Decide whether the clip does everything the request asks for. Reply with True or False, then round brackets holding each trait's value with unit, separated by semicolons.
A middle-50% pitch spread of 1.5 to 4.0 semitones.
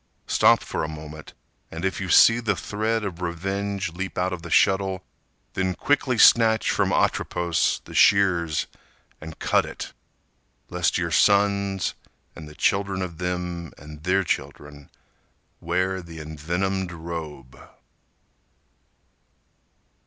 True (3.0 semitones)